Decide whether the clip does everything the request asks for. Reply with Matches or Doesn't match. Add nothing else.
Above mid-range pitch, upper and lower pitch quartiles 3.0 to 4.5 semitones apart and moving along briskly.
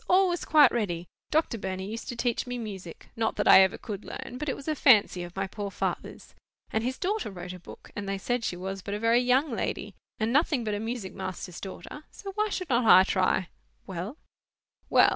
Doesn't match